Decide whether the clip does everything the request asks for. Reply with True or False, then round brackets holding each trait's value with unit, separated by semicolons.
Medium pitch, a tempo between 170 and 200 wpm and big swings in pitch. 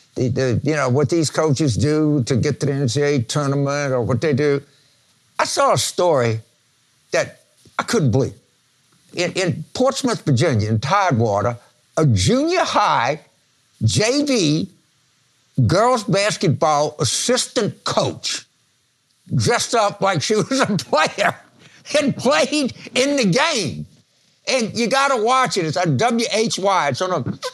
False (155 Hz; 140 wpm; 9.0 semitones)